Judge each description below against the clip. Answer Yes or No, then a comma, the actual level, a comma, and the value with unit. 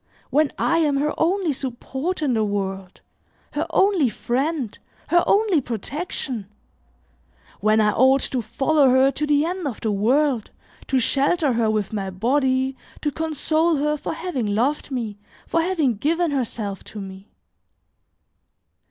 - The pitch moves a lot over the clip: Yes, wide, 6.0 semitones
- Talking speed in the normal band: Yes, average, 145 wpm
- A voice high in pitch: Yes, very high, 270 Hz